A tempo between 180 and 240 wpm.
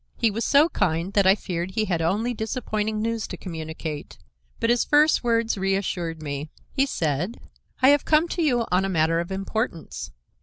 Yes: average, 185 wpm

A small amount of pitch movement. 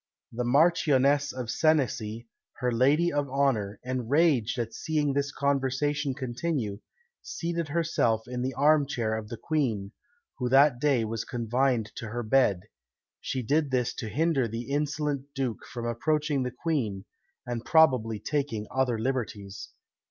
No: average, 3.8 semitones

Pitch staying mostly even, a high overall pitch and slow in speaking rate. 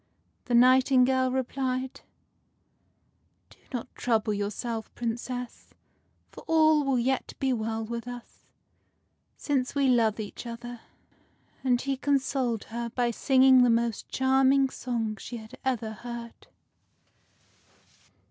Yes: narrow, 2.2 semitones; high, 245 Hz; slow, 120 wpm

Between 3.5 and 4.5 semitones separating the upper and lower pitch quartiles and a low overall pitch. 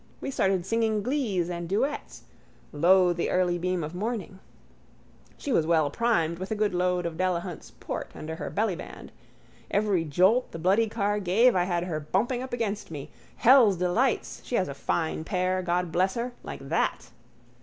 No: average, 4.1 semitones; medium, 185 Hz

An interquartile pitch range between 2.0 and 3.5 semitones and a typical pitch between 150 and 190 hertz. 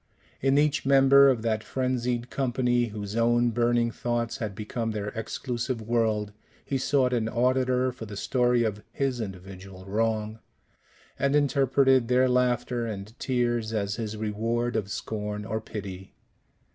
No: average, 2.8 semitones; low, 120 Hz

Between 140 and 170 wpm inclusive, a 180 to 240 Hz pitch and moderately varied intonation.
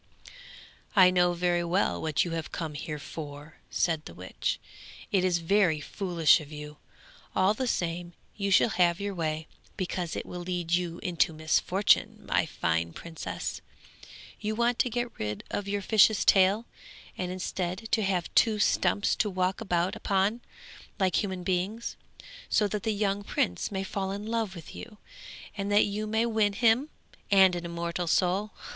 Yes: average, 165 wpm; medium, 185 Hz; average, 3.3 semitones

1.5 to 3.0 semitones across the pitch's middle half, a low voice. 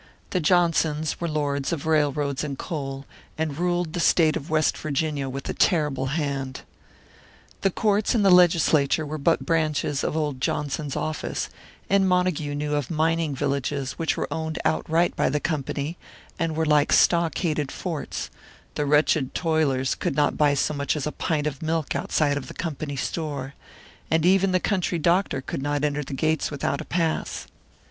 No: narrow, 2.5 semitones; medium, 155 Hz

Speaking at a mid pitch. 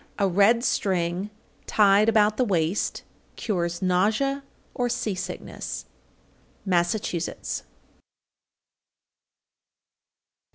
No: high, 200 Hz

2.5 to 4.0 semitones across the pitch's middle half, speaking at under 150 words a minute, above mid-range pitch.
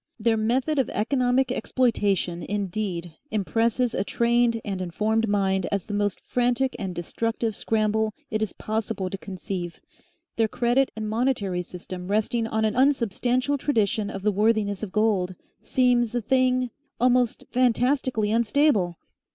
Yes: average, 3.5 semitones; average, 140 wpm; high, 220 Hz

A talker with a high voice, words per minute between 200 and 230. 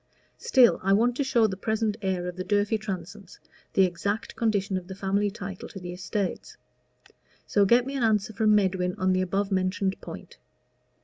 No: high, 200 Hz; average, 185 wpm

